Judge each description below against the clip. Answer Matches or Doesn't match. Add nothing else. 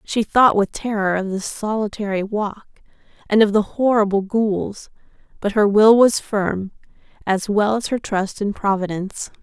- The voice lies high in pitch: Matches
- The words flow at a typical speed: Matches